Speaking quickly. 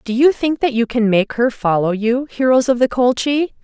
Yes: fast, 230 wpm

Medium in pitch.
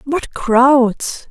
No: very high, 260 Hz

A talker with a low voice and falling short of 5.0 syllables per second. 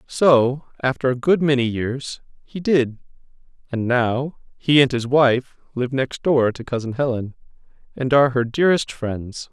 Yes: low, 130 Hz; 4.3 syllables/s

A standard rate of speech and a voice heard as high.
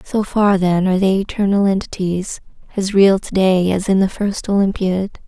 Yes: average, 180 wpm; high, 195 Hz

